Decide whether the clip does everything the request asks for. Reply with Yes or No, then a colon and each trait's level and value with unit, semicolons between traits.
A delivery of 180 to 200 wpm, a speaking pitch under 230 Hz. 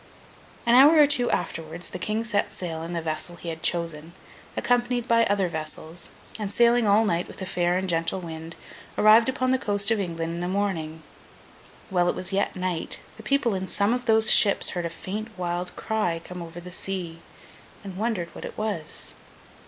Yes: average, 195 wpm; medium, 185 Hz